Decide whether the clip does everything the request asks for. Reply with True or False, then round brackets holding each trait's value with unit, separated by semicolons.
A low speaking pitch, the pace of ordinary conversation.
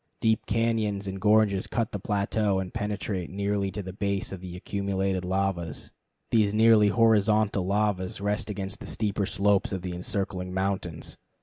True (100 Hz; 160 wpm)